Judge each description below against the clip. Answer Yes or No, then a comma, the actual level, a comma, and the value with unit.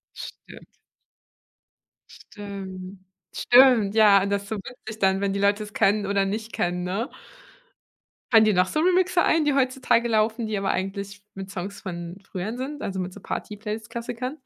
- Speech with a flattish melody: No, average, 3.1 semitones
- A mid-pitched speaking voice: No, high, 205 Hz